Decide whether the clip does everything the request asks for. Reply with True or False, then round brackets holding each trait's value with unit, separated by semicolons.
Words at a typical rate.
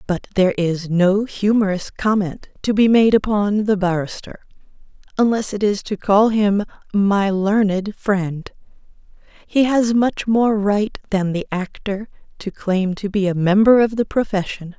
True (150 wpm)